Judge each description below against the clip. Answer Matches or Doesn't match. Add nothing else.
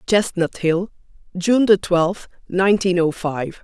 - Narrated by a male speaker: Doesn't match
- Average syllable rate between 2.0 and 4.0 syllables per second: Matches